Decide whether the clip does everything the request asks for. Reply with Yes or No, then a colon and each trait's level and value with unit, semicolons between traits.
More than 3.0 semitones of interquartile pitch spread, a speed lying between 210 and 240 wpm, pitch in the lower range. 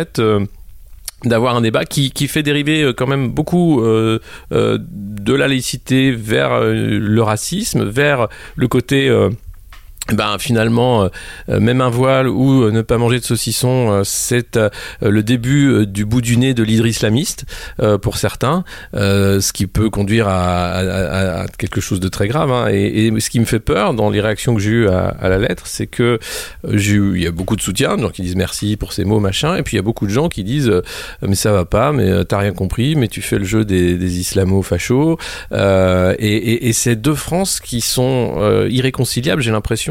Yes: average, 4.0 semitones; average, 215 wpm; low, 110 Hz